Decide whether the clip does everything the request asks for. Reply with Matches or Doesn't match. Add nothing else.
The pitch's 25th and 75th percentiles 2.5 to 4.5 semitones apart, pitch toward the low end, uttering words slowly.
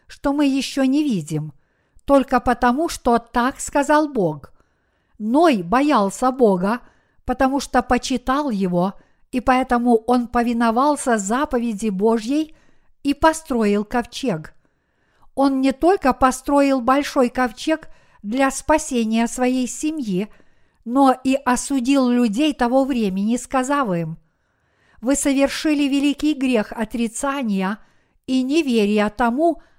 Doesn't match